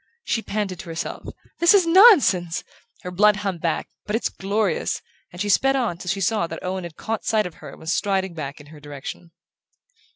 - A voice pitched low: No, high, 190 Hz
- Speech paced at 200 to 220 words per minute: Yes, fast, 205 wpm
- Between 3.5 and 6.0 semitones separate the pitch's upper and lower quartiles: Yes, average, 4.2 semitones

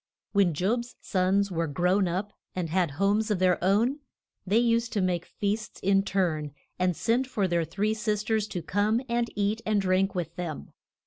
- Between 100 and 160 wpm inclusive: No, average, 185 wpm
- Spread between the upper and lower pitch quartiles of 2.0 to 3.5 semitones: Yes, average, 3.1 semitones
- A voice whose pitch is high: Yes, high, 195 Hz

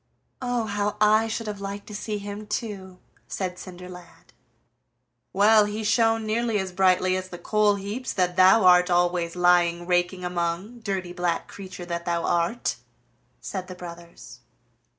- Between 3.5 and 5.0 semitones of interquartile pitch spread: No, average, 2.9 semitones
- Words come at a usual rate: Yes, average, 150 wpm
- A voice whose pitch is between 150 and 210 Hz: Yes, medium, 185 Hz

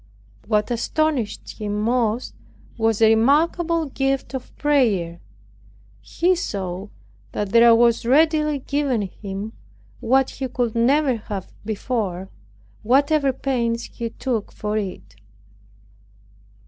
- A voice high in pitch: Yes, high, 235 Hz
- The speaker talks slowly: Yes, slow, 110 wpm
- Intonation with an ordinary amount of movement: Yes, average, 4.5 semitones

